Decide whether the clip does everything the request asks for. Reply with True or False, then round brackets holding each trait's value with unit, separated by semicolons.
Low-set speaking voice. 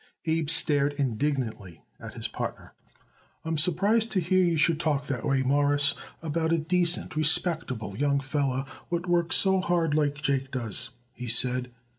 False (145 Hz)